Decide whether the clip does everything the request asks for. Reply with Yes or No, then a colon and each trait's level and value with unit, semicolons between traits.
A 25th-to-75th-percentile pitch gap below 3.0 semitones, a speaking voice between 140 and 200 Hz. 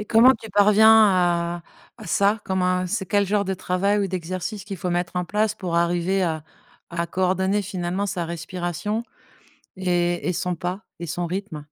Yes: narrow, 2.5 semitones; medium, 185 Hz